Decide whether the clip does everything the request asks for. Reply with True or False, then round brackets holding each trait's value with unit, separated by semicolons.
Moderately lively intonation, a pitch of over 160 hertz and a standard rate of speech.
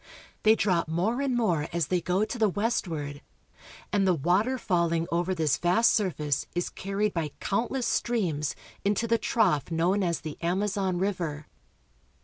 True (4.2 semitones; 185 Hz; 155 wpm)